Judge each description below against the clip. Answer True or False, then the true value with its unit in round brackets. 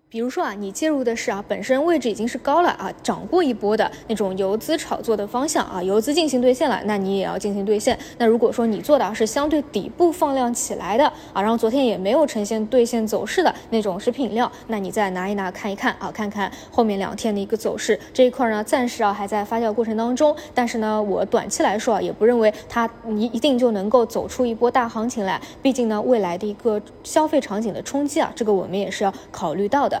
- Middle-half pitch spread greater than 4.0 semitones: False (3.6 semitones)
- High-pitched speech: True (230 Hz)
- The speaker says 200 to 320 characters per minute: False (355 characters per minute)